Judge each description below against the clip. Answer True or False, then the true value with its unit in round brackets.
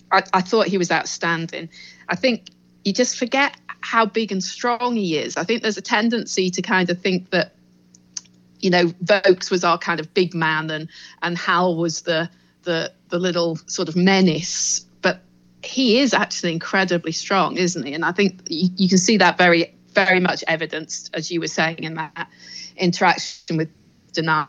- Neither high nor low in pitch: True (175 Hz)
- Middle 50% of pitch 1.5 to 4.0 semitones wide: True (3.1 semitones)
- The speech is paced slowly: False (185 wpm)